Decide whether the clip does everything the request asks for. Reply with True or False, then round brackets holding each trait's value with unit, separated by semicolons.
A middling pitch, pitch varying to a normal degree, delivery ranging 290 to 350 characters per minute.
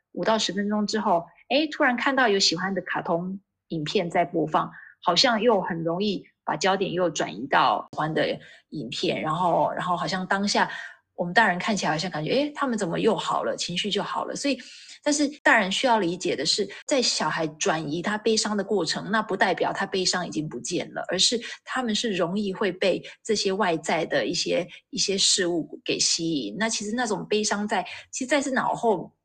False (200 Hz; 4.2 semitones; 300 characters per minute)